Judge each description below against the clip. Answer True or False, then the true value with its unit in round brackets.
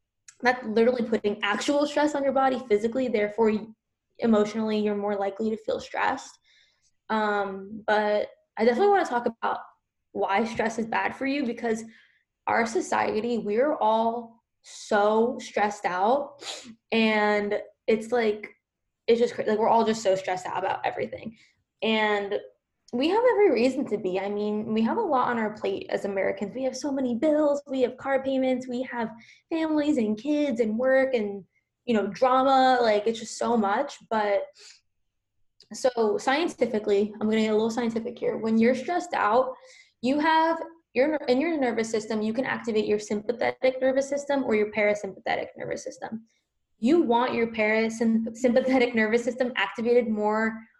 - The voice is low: False (230 Hz)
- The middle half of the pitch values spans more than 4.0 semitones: False (3.6 semitones)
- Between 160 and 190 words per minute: True (165 wpm)